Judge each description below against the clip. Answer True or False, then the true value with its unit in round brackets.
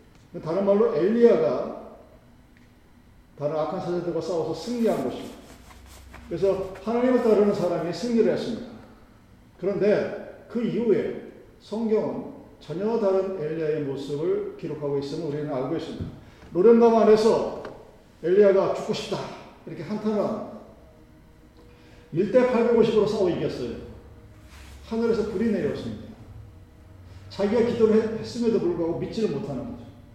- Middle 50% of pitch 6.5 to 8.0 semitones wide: True (6.9 semitones)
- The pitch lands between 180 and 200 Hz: True (190 Hz)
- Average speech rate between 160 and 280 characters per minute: False (295 characters per minute)